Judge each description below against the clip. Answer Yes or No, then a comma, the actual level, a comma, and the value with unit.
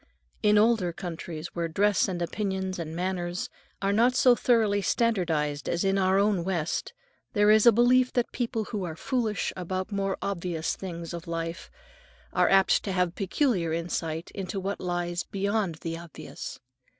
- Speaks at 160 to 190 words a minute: Yes, average, 165 wpm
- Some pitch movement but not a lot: Yes, average, 3.4 semitones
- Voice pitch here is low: No, high, 190 Hz